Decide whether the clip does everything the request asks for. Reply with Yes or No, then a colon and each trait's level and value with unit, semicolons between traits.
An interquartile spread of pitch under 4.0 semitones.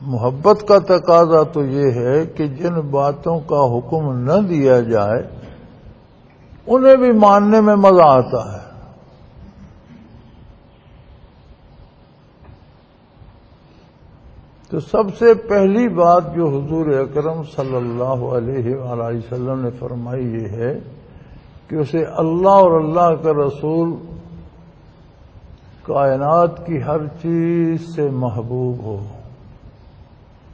No: wide, 5.4 semitones